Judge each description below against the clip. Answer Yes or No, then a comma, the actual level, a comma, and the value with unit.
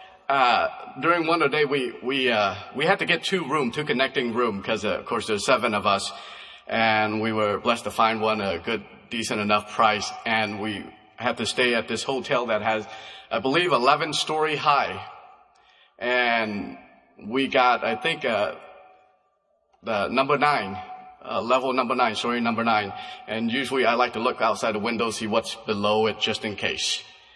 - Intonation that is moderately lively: Yes, average, 5.0 semitones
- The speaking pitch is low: Yes, low, 115 Hz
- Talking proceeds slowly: No, average, 180 wpm